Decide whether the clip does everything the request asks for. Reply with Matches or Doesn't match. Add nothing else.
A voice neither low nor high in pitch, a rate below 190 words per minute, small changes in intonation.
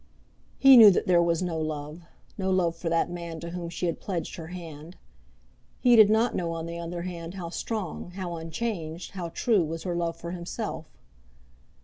Doesn't match